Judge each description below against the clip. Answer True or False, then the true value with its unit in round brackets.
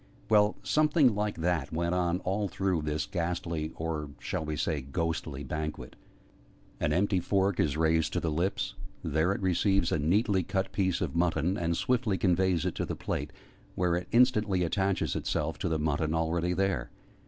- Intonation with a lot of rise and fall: False (3.3 semitones)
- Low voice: True (85 Hz)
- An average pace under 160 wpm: False (175 wpm)